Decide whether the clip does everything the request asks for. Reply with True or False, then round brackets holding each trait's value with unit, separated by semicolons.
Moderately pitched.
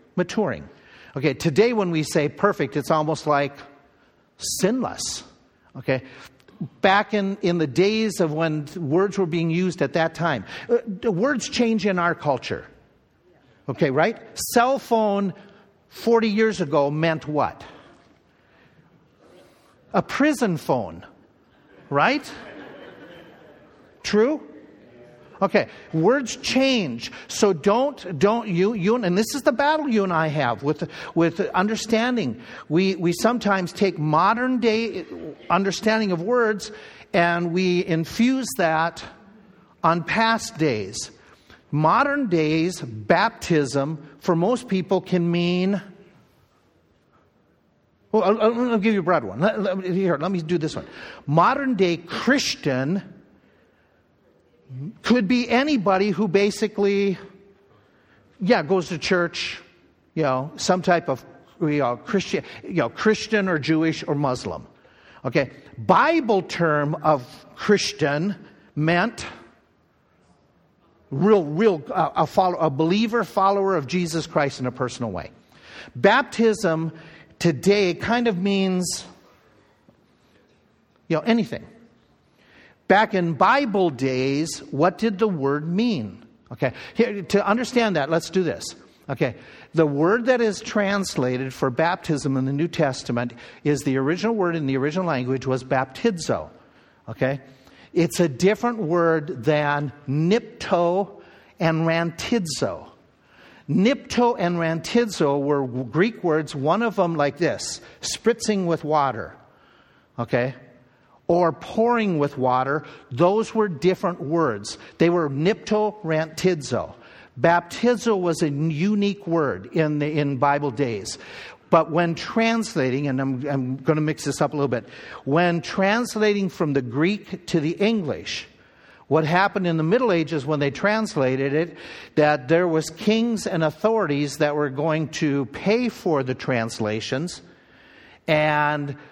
True (170 Hz)